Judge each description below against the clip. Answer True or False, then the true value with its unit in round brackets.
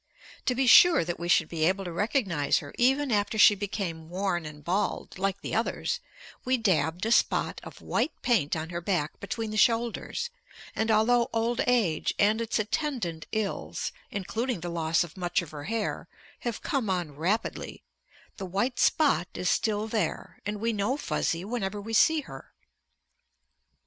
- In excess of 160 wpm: True (170 wpm)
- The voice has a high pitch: True (205 Hz)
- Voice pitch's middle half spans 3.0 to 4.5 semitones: False (5.0 semitones)